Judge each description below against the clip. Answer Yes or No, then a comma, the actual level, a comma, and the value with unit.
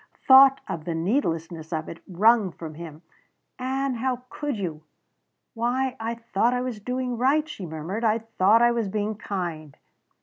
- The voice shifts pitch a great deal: Yes, wide, 6.6 semitones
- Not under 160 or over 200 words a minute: Yes, average, 165 wpm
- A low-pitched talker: No, high, 225 Hz